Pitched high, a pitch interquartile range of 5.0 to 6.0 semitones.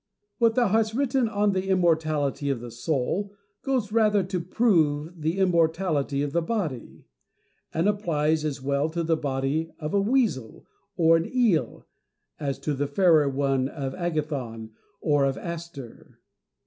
No: medium, 160 Hz; wide, 5.4 semitones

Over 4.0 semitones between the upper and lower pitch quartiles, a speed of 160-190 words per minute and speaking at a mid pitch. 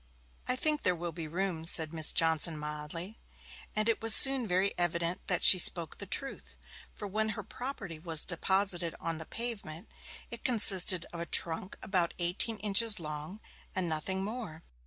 Yes: average, 4.4 semitones; average, 170 wpm; medium, 180 Hz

